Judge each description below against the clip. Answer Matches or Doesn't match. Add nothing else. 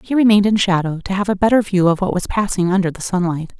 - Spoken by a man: Doesn't match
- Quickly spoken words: Matches